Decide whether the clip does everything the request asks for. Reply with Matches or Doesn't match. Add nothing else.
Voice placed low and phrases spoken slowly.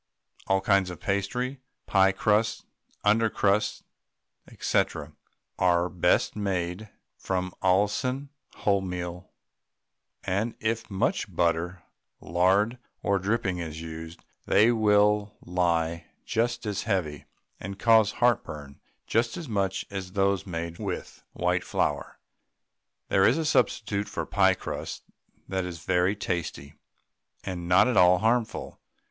Matches